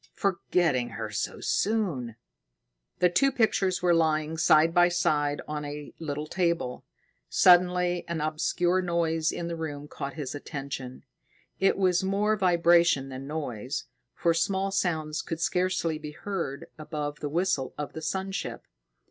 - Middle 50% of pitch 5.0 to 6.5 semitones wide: No, average, 3.3 semitones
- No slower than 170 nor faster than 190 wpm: No, average, 145 wpm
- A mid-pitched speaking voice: Yes, medium, 165 Hz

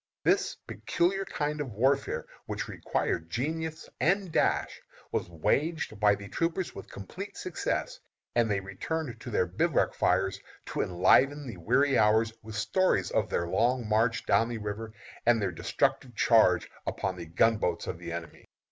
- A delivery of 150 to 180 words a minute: Yes, average, 155 wpm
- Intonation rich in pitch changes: Yes, wide, 7.1 semitones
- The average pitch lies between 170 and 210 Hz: No, low, 115 Hz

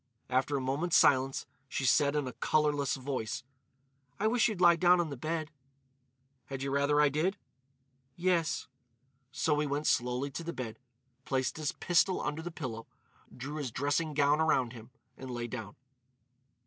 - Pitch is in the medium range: Yes, medium, 145 Hz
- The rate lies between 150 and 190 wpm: Yes, average, 165 wpm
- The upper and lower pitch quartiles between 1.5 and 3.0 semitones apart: No, average, 3.6 semitones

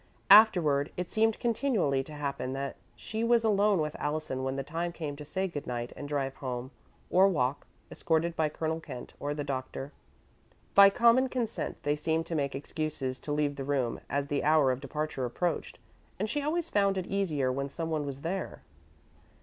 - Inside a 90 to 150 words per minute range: No, average, 185 wpm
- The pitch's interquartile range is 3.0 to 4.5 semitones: No, wide, 5.4 semitones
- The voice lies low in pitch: No, medium, 150 Hz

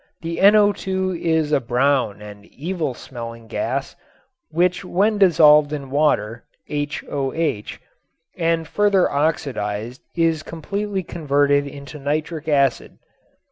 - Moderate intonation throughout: Yes, average, 3.8 semitones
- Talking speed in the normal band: No, slow, 105 wpm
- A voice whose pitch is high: No, medium, 150 Hz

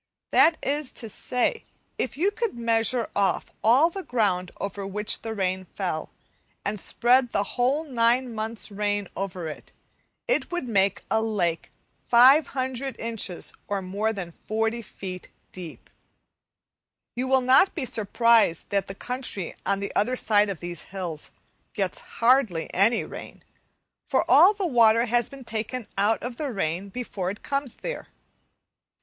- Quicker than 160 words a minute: No, average, 150 wpm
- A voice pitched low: No, high, 225 Hz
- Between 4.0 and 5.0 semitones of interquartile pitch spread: Yes, average, 4.5 semitones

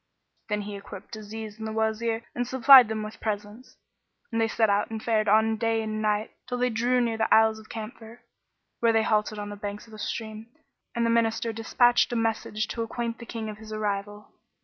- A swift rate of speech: Yes, fast, 215 wpm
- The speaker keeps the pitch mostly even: Yes, narrow, 1.2 semitones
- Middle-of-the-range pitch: No, high, 220 Hz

